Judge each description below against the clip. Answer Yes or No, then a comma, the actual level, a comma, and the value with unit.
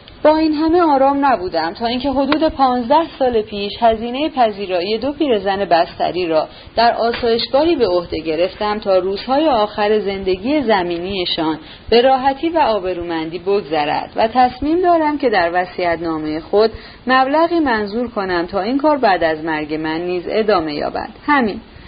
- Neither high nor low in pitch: No, high, 220 Hz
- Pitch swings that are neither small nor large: No, wide, 7.3 semitones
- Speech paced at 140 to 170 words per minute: Yes, average, 150 wpm